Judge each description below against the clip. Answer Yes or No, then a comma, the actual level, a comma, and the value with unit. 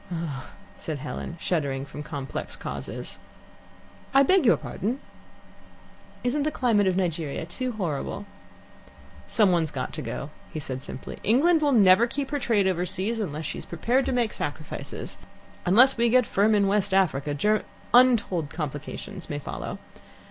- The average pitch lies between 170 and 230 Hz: Yes, high, 190 Hz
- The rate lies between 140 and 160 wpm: Yes, average, 155 wpm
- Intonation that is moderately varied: No, wide, 7.5 semitones